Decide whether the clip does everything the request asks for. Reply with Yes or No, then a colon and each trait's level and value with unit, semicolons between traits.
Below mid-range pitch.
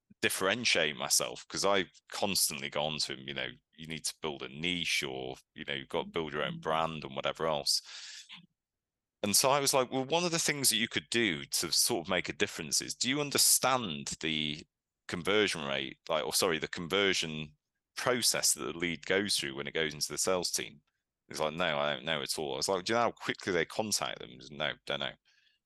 Yes: very low, 80 Hz